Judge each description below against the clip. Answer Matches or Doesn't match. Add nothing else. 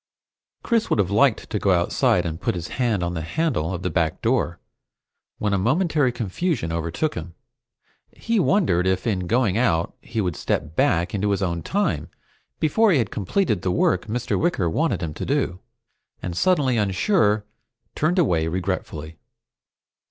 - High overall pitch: Doesn't match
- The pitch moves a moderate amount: Doesn't match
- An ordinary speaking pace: Matches